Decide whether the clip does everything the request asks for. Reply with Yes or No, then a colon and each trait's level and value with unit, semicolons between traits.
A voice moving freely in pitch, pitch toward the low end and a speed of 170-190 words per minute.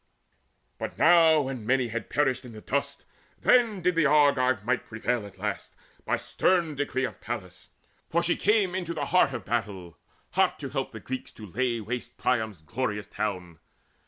Yes: wide, 6.0 semitones; low, 130 Hz; average, 175 wpm